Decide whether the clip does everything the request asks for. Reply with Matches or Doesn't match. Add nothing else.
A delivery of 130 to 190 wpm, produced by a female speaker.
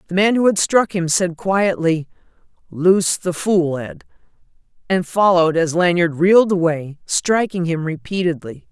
Matches